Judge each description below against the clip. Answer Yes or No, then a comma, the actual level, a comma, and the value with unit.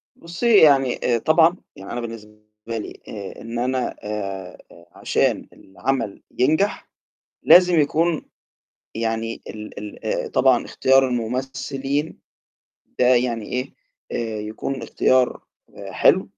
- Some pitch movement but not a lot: Yes, average, 3.9 semitones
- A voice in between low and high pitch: No, low, 125 Hz